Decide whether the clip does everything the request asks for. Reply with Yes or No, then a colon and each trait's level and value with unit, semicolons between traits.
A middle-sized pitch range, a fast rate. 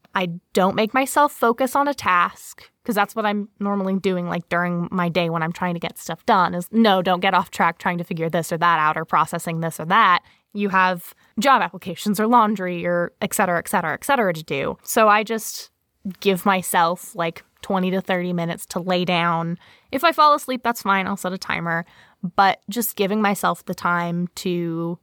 Yes: average, 3.4 semitones; fast, 215 wpm